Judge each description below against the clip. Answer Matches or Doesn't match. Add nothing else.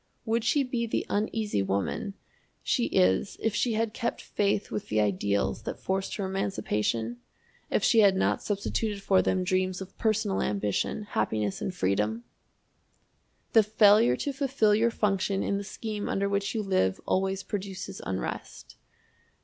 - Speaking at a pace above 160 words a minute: Doesn't match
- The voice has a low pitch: Doesn't match